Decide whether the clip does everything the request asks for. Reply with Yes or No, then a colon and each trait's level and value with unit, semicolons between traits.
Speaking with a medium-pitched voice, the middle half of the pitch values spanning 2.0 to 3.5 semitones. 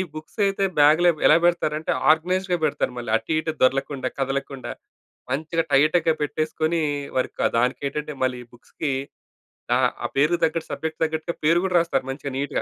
Yes: medium, 155 Hz; average, 3.2 semitones